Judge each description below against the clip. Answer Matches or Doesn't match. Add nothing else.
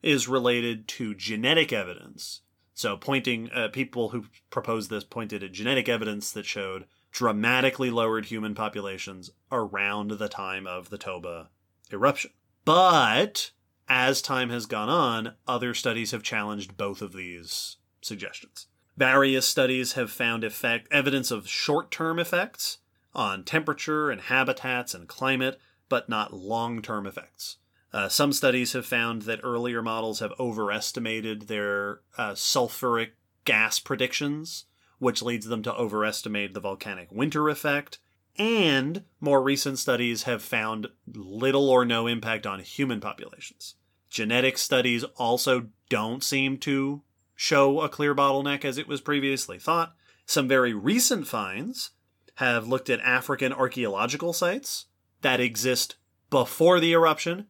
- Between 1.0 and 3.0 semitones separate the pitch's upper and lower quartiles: Doesn't match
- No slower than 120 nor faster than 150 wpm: Matches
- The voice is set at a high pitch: Doesn't match